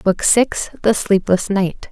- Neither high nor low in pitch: No, high, 200 Hz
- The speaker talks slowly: Yes, slow, 125 wpm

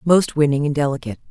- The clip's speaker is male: No, female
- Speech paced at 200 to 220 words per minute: No, average, 185 wpm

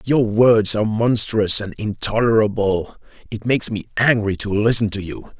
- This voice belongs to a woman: No, male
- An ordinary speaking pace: Yes, average, 155 wpm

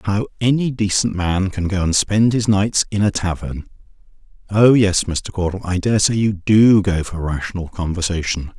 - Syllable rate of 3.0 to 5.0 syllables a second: Yes, 4.9 syllables/s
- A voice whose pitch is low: Yes, very low, 95 Hz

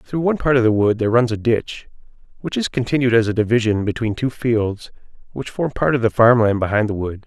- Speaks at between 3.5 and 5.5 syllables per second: No, 5.9 syllables/s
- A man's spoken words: Yes, male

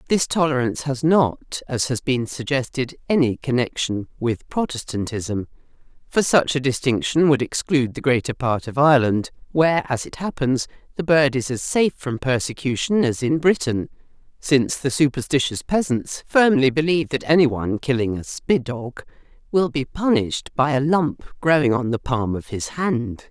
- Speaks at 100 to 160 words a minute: Yes, average, 155 wpm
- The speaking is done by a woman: Yes, female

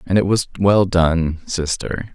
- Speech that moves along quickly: No, average, 140 wpm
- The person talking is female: No, male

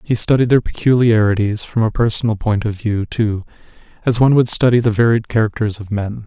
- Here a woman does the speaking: No, male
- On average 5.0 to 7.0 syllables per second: Yes, 5.7 syllables/s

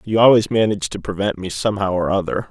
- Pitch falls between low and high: No, low, 100 Hz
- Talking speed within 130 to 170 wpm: No, fast, 215 wpm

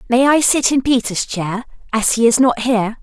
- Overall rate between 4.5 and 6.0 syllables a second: Yes, 5.1 syllables/s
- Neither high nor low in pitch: No, high, 240 Hz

